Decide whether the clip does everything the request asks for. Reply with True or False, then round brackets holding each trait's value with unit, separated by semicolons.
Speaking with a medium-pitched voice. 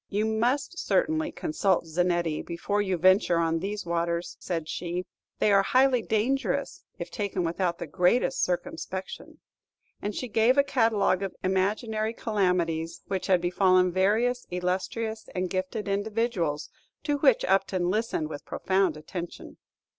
False (195 Hz)